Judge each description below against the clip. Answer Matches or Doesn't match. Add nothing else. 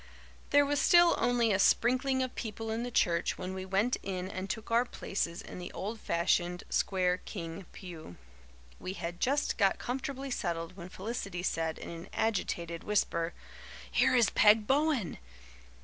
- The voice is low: Doesn't match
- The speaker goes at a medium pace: Matches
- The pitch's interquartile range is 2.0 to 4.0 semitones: Doesn't match